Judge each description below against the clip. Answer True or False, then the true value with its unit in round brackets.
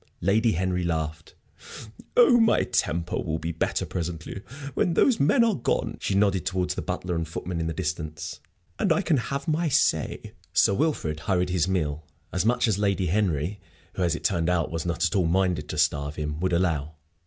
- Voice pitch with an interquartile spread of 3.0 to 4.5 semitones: True (4.1 semitones)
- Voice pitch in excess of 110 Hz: False (90 Hz)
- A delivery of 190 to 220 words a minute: True (195 wpm)